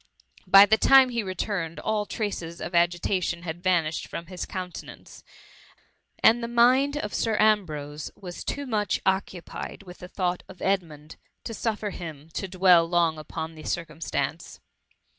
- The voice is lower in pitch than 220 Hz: Yes, medium, 185 Hz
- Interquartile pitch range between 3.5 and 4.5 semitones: Yes, average, 3.9 semitones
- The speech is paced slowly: No, average, 150 wpm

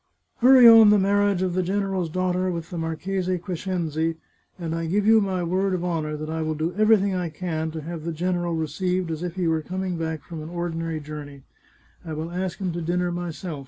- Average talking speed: No, fast, 220 wpm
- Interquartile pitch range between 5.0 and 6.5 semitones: No, narrow, 2.5 semitones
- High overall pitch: No, medium, 175 Hz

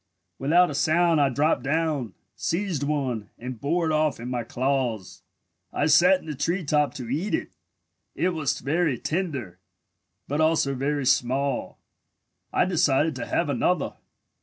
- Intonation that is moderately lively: Yes, average, 3.6 semitones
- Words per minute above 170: No, average, 155 wpm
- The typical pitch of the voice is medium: Yes, medium, 145 Hz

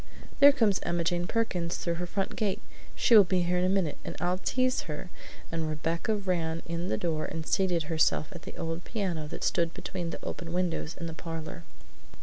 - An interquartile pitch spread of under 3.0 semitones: Yes, narrow, 2.4 semitones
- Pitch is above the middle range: No, medium, 175 Hz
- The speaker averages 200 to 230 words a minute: Yes, fast, 205 wpm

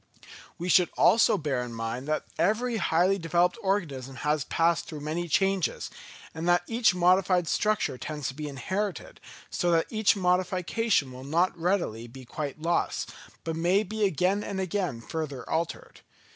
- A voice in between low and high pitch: Yes, medium, 170 Hz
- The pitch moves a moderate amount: Yes, average, 4.3 semitones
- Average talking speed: Yes, average, 160 wpm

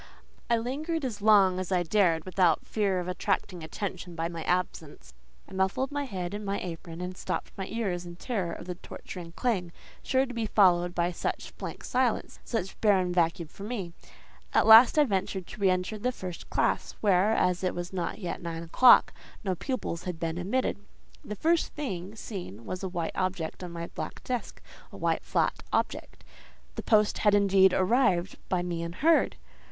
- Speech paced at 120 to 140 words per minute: No, average, 185 wpm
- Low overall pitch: No, medium, 185 Hz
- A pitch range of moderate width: Yes, average, 3.6 semitones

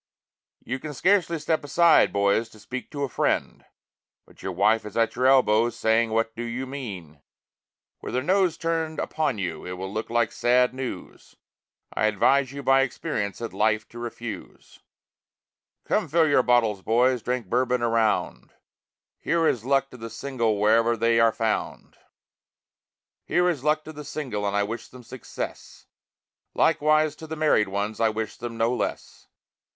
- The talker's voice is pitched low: Yes, low, 120 Hz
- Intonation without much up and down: No, average, 4.1 semitones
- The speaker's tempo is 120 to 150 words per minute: No, average, 170 wpm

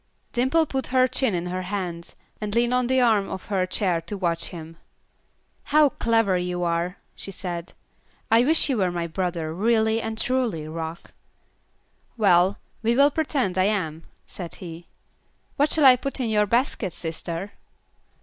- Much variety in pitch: Yes, wide, 5.7 semitones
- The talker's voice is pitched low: No, high, 200 Hz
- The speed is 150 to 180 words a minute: Yes, average, 165 wpm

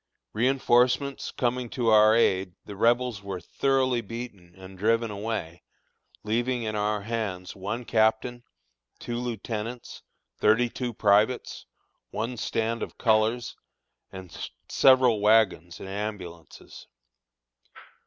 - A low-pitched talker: Yes, low, 110 Hz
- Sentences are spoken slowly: Yes, slow, 110 wpm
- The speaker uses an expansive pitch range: No, average, 3.0 semitones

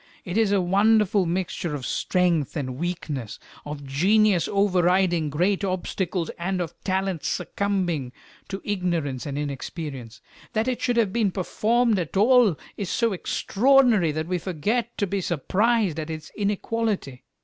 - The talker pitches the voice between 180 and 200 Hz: Yes, medium, 185 Hz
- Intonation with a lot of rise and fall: No, average, 4.5 semitones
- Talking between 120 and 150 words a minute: Yes, average, 145 wpm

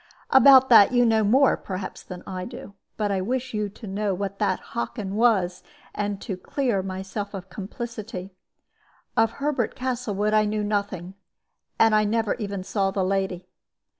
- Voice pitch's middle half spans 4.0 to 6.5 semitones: No, average, 2.9 semitones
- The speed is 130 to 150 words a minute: No, average, 165 wpm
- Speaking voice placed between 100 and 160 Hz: No, high, 205 Hz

